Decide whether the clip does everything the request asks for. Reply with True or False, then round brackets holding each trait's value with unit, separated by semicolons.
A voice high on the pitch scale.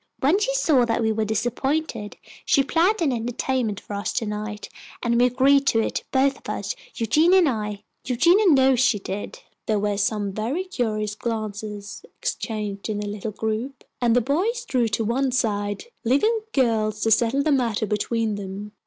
True (230 Hz)